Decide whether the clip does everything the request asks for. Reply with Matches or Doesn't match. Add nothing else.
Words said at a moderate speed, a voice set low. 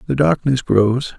Matches